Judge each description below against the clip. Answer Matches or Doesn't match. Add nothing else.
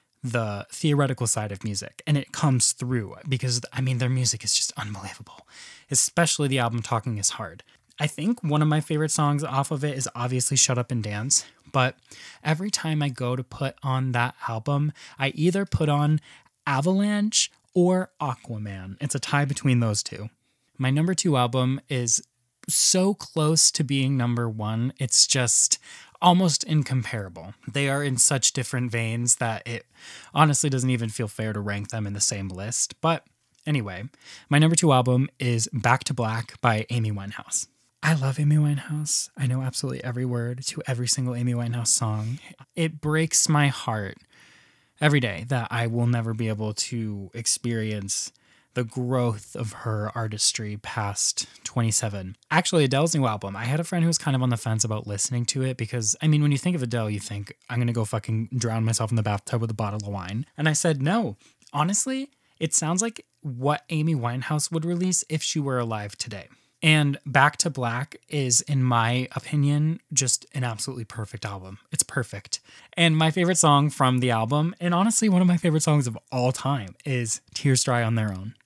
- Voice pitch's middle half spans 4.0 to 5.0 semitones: Matches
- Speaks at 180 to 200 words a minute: Matches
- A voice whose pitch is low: Matches